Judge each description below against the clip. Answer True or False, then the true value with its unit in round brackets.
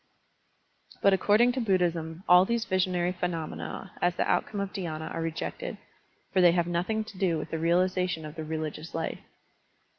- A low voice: False (180 Hz)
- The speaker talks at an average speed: True (170 wpm)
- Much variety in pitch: False (2.7 semitones)